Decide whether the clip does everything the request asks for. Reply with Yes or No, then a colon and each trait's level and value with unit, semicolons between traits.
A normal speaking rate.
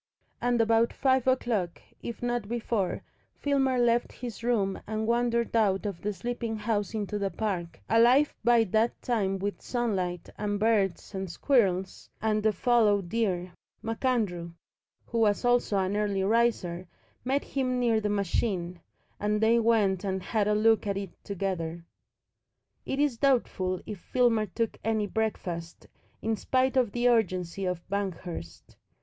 Yes: average, 150 wpm